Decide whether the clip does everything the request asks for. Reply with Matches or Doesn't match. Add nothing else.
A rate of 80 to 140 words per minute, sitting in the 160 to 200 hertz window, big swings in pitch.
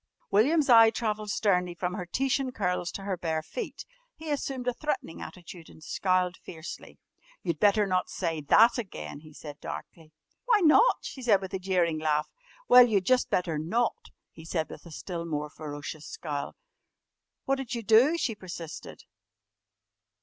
Doesn't match